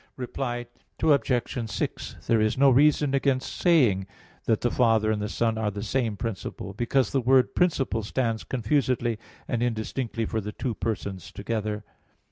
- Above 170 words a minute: No, average, 155 wpm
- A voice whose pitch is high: No, low, 115 Hz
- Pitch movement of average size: Yes, average, 3.3 semitones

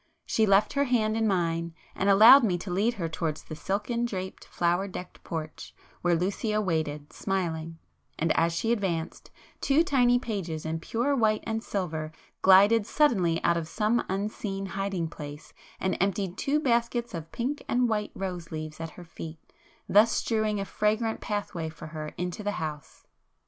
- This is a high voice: Yes, high, 195 Hz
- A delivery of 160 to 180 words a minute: Yes, average, 165 wpm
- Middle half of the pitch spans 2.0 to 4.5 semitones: No, average, 5.0 semitones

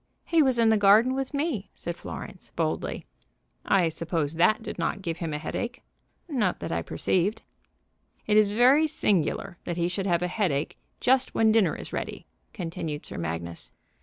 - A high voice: Yes, high, 195 Hz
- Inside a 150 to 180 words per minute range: Yes, average, 175 wpm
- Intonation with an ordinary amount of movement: No, wide, 5.8 semitones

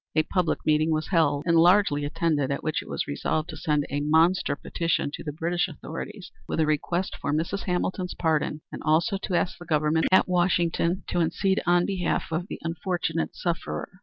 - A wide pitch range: No, narrow, 2.5 semitones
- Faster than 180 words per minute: Yes, average, 195 wpm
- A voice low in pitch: No, medium, 165 Hz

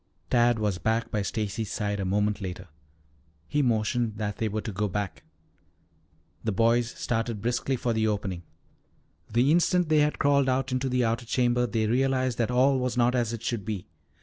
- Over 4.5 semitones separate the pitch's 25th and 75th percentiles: No, average, 3.2 semitones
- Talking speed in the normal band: Yes, average, 185 wpm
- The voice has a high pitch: No, low, 115 Hz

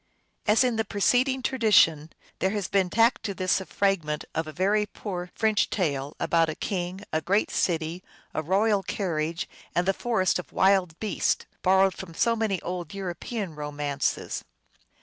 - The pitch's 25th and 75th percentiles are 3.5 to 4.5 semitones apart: Yes, average, 4.1 semitones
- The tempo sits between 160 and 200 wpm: Yes, average, 170 wpm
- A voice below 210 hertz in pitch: Yes, high, 190 Hz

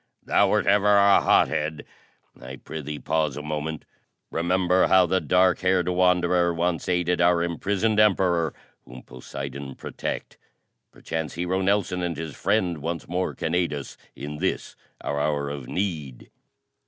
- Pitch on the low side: Yes, very low, 85 Hz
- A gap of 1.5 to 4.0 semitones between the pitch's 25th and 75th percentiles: Yes, average, 3.6 semitones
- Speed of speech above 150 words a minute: No, average, 145 wpm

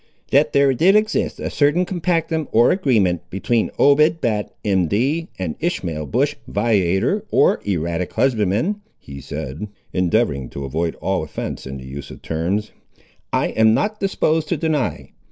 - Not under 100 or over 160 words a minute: Yes, average, 150 wpm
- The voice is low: Yes, low, 110 Hz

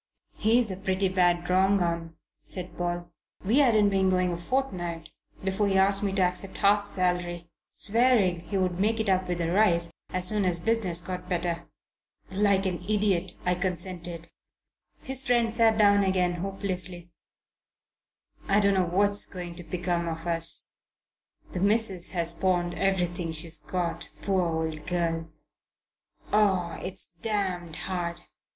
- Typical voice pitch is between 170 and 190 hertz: Yes, medium, 185 Hz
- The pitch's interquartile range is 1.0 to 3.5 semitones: Yes, narrow, 2.4 semitones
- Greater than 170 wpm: No, average, 150 wpm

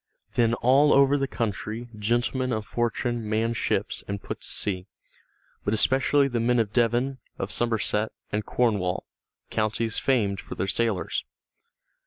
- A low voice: Yes, low, 115 Hz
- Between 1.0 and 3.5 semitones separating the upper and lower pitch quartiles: Yes, narrow, 2.6 semitones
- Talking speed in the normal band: Yes, average, 145 wpm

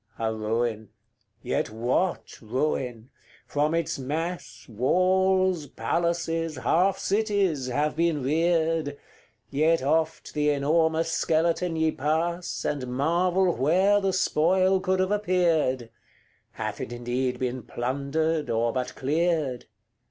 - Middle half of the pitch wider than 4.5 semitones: Yes, average, 4.9 semitones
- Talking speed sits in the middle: No, slow, 115 wpm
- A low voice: No, medium, 160 Hz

